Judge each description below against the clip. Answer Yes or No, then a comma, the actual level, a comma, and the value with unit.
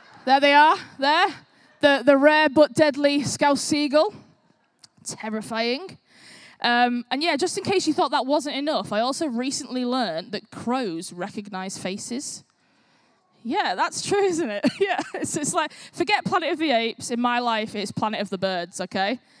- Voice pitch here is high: Yes, very high, 270 Hz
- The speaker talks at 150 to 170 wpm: Yes, average, 165 wpm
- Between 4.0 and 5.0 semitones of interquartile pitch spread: No, wide, 5.6 semitones